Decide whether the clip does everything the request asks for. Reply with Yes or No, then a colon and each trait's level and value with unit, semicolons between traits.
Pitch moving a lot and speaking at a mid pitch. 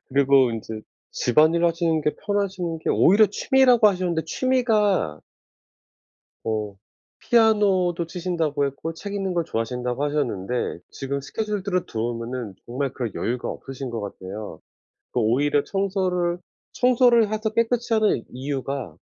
Yes: wide, 8.3 semitones; medium, 165 Hz